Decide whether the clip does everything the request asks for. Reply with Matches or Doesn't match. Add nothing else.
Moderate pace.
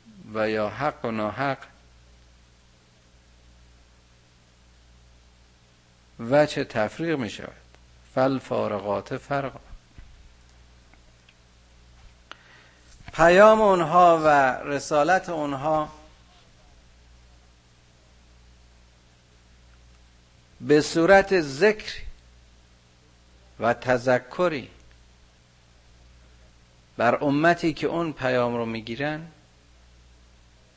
Doesn't match